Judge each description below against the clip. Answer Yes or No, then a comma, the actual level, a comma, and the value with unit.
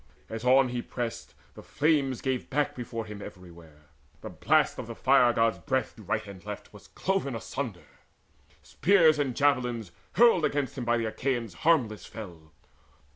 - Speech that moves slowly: No, average, 165 wpm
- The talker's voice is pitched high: No, low, 120 Hz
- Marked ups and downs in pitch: No, average, 4.5 semitones